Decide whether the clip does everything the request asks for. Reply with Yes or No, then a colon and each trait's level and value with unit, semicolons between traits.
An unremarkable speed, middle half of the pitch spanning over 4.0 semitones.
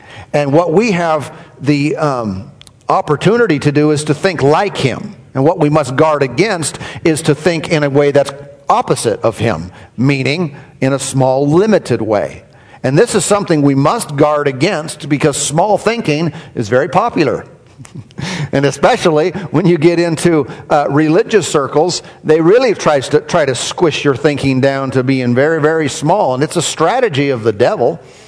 No: average, 170 wpm; average, 3.0 semitones